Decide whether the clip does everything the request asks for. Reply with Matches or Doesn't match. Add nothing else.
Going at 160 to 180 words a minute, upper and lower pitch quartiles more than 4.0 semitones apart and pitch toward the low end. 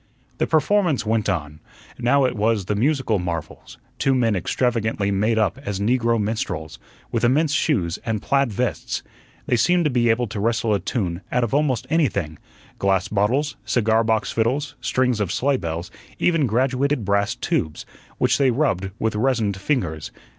Matches